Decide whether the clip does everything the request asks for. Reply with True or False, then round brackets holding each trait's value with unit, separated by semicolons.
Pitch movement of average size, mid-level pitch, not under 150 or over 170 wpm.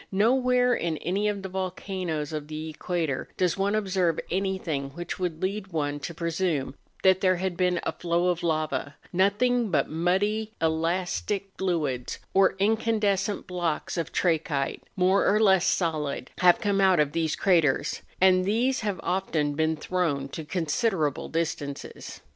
True (3.6 semitones; 180 Hz; 155 wpm)